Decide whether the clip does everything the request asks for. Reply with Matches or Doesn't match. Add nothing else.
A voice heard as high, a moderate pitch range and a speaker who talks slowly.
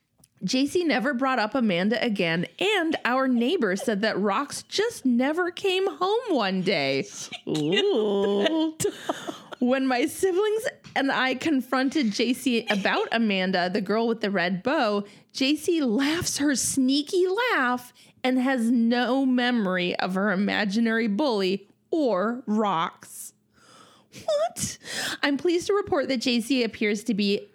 Doesn't match